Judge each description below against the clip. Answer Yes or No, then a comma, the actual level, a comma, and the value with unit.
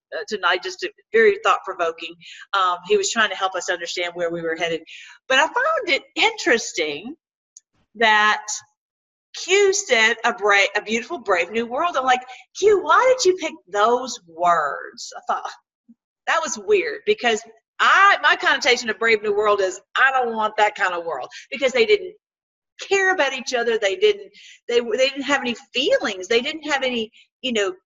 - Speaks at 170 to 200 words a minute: Yes, average, 180 wpm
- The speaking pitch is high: Yes, high, 245 Hz